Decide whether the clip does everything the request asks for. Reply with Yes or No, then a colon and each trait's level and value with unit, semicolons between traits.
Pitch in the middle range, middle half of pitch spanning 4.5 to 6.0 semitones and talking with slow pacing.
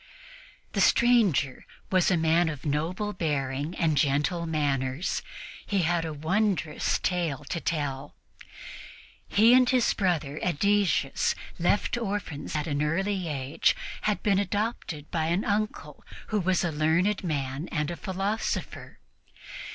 Yes: medium, 170 Hz; average, 5.1 semitones; slow, 130 wpm